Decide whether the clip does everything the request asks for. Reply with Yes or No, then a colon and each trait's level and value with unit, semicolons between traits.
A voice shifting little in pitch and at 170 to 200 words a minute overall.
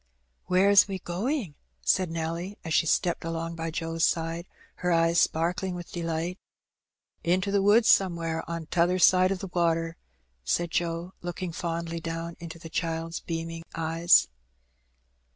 No: narrow, 1.7 semitones; average, 150 wpm